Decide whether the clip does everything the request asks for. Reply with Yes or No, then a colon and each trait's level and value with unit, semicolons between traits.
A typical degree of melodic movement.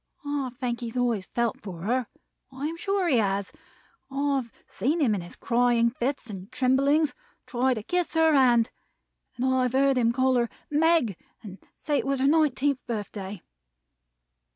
Yes: average, 3.4 semitones